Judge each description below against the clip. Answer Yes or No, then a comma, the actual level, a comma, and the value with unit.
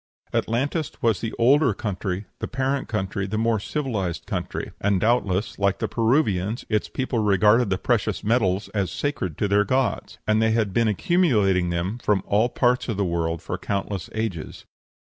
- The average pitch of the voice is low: Yes, low, 105 Hz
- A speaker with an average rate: Yes, average, 170 wpm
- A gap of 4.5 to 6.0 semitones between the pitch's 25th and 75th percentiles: No, average, 3.8 semitones